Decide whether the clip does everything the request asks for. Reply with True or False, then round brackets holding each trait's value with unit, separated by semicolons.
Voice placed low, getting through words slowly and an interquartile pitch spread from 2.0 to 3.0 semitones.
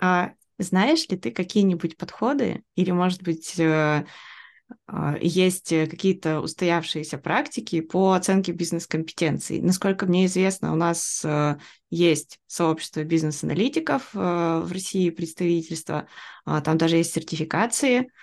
False (175 Hz; 100 wpm; 2.7 semitones)